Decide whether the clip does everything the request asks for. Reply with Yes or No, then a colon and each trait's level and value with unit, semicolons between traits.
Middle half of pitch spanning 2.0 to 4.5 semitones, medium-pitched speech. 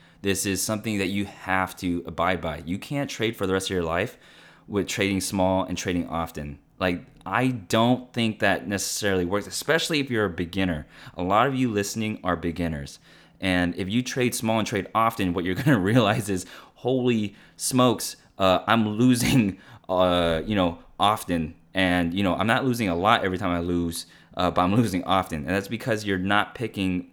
No: average, 3.9 semitones; very low, 95 Hz